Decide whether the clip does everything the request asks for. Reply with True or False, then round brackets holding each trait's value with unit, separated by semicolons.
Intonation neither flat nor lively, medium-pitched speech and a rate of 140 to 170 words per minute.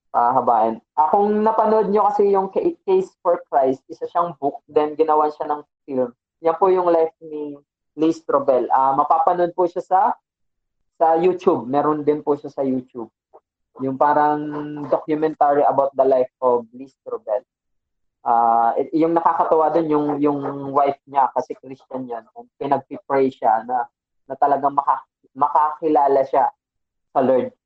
True (4.3 semitones; 150 Hz; 155 wpm)